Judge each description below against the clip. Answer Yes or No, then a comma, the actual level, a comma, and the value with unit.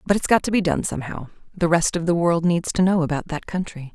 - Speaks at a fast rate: Yes, fast, 275 wpm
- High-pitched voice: No, medium, 170 Hz